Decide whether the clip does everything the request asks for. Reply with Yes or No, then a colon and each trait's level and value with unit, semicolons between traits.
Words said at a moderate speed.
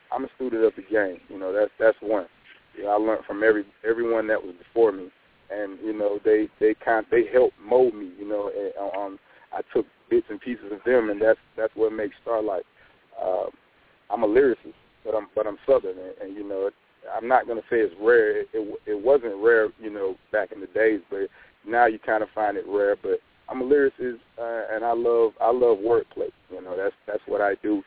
No: fast, 230 wpm